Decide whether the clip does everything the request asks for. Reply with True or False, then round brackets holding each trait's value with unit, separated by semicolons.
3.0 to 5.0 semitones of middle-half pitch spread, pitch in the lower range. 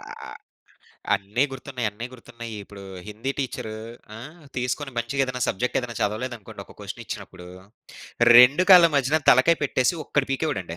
True (3.8 semitones; 125 Hz)